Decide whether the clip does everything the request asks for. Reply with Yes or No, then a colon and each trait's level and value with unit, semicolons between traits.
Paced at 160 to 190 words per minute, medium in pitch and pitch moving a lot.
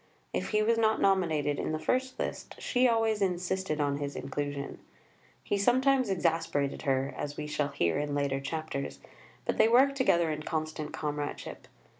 Yes: average, 165 wpm; medium, 160 Hz; wide, 6.8 semitones